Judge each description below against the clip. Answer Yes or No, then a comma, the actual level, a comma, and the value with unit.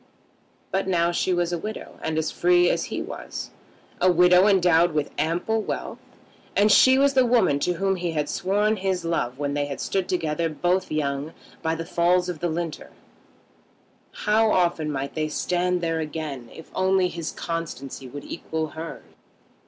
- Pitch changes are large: No, average, 3.0 semitones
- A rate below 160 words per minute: No, average, 175 wpm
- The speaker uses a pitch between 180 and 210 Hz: No, medium, 170 Hz